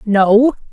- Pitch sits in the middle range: No, high, 225 Hz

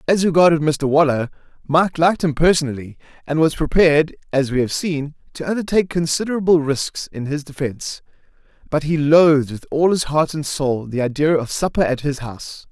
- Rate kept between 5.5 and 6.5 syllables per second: Yes, 5.6 syllables/s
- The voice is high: No, medium, 150 Hz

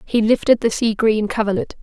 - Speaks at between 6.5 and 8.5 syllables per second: No, 5.4 syllables/s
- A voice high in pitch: Yes, high, 215 Hz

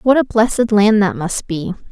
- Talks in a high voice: Yes, high, 215 Hz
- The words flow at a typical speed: No, fast, 220 wpm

